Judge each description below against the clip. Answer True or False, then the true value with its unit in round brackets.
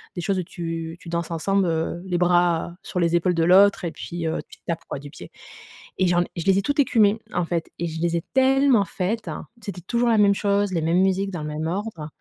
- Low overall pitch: False (175 Hz)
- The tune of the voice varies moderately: True (3.1 semitones)